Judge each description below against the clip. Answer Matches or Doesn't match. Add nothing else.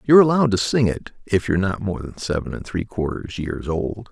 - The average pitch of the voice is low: Matches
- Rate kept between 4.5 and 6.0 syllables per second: Doesn't match